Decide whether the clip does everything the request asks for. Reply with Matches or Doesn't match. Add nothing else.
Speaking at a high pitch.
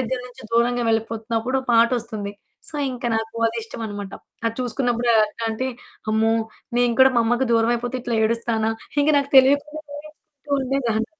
Matches